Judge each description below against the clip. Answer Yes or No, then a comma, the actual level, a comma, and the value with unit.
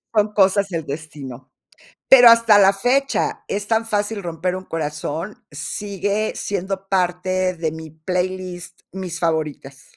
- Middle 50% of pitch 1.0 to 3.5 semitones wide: No, average, 4.0 semitones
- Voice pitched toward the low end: No, medium, 185 Hz